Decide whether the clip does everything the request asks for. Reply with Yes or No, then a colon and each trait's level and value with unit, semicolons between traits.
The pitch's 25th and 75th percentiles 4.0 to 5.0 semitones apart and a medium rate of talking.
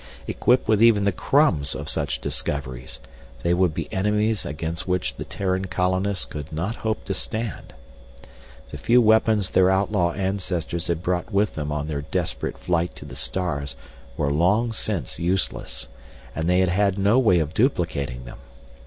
Yes: average, 4.3 semitones; average, 165 wpm